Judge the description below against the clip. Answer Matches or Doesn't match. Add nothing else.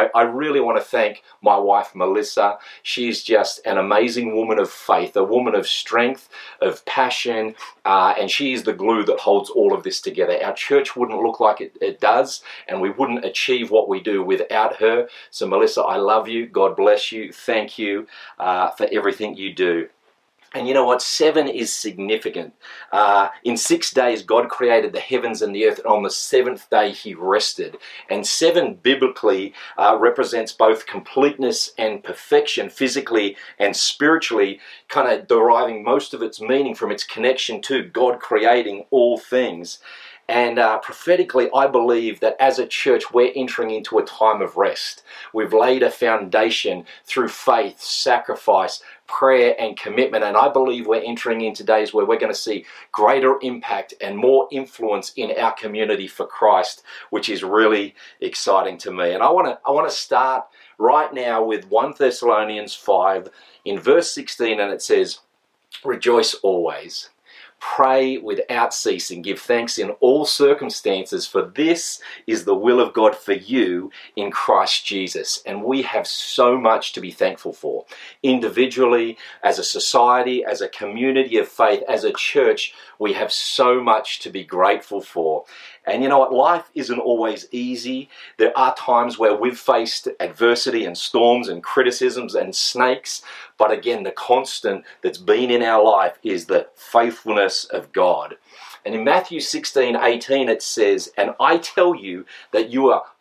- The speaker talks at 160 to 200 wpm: Matches